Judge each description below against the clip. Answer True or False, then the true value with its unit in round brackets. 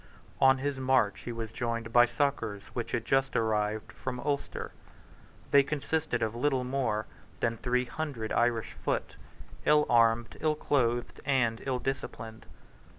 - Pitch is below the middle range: True (120 Hz)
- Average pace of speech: True (145 wpm)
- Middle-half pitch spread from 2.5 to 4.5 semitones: True (2.9 semitones)